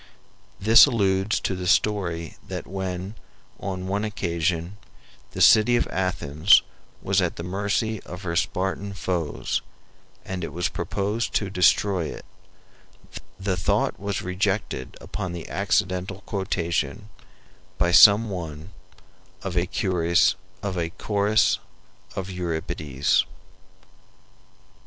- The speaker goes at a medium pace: No, slow, 110 wpm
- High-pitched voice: No, very low, 95 Hz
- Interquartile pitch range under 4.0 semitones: Yes, average, 2.7 semitones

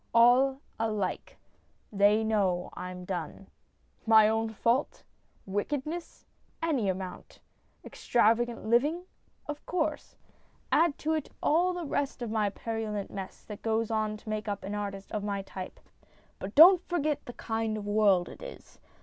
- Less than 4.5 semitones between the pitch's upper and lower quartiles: No, average, 5.1 semitones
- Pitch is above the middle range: Yes, high, 220 Hz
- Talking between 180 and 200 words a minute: No, average, 140 wpm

